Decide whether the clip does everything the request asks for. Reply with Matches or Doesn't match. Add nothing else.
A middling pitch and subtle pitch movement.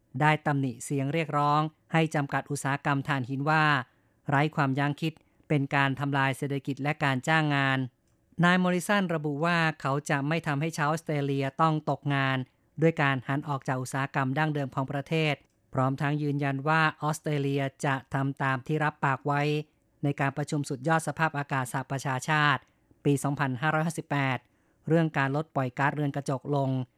Matches